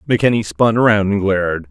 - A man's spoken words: Yes, male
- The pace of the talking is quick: No, average, 175 wpm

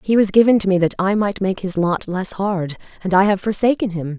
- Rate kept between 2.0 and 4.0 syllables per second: No, 5.5 syllables/s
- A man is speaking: No, female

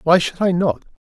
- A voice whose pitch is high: No, medium, 175 Hz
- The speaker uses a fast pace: Yes, fast, 225 wpm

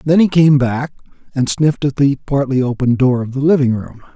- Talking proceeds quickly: Yes, fast, 215 wpm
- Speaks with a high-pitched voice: No, low, 135 Hz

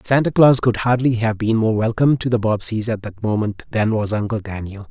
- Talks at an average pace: No, fast, 220 wpm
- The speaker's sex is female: No, male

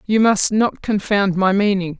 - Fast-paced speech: No, average, 180 wpm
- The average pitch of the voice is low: No, high, 200 Hz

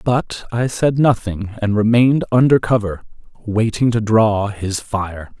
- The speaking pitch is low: Yes, low, 110 Hz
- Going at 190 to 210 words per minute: No, average, 145 wpm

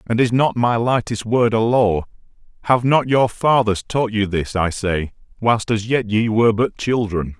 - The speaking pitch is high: No, low, 110 Hz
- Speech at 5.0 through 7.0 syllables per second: No, 4.4 syllables/s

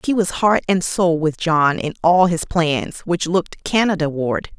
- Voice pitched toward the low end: No, medium, 170 Hz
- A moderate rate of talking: Yes, average, 195 wpm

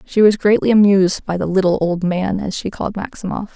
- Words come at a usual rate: No, fast, 220 wpm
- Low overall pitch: No, high, 195 Hz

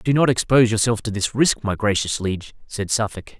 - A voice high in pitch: No, low, 110 Hz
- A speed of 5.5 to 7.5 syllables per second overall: Yes, 5.6 syllables/s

